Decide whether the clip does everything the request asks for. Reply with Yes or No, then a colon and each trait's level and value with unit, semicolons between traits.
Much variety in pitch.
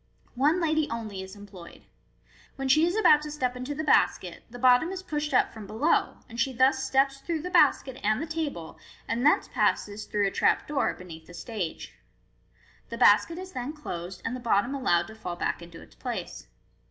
Yes: wide, 6.7 semitones